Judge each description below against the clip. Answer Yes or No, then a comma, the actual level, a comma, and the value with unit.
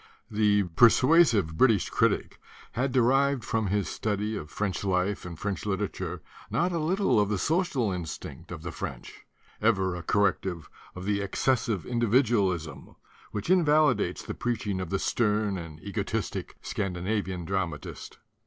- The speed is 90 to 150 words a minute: Yes, average, 145 wpm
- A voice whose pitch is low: Yes, low, 105 Hz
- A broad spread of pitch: No, average, 4.4 semitones